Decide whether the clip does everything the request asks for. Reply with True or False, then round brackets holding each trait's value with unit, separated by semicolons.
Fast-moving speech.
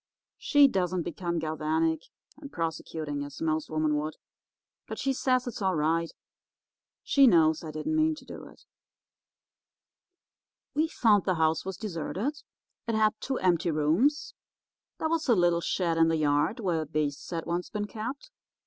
False (160 wpm)